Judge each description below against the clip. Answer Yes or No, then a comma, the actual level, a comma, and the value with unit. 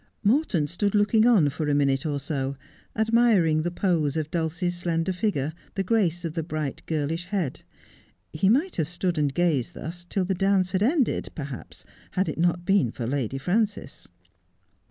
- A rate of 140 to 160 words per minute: No, average, 175 wpm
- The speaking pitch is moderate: Yes, medium, 175 Hz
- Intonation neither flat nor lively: Yes, average, 4.6 semitones